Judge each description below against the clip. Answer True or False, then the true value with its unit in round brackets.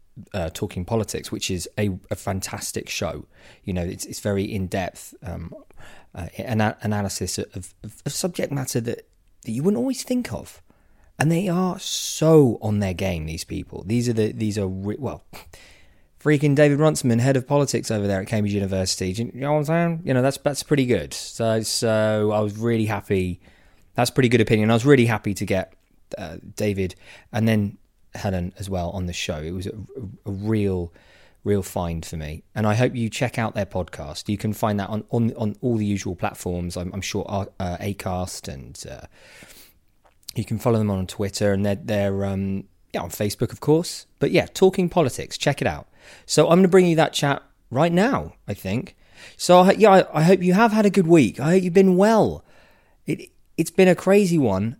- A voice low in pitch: True (105 Hz)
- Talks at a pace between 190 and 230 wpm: True (195 wpm)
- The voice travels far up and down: True (6.3 semitones)